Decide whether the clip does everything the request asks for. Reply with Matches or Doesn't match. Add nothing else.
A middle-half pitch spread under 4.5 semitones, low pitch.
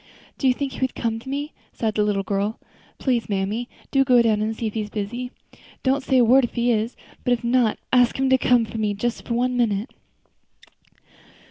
Doesn't match